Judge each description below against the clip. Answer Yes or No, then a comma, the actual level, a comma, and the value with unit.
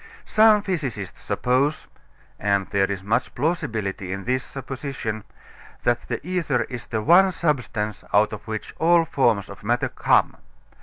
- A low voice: Yes, low, 125 Hz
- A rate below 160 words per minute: Yes, average, 145 wpm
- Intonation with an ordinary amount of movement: No, wide, 6.9 semitones